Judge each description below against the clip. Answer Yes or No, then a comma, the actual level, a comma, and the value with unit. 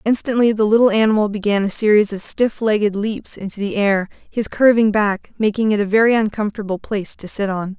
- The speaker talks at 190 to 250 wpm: Yes, average, 200 wpm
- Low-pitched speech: No, high, 210 Hz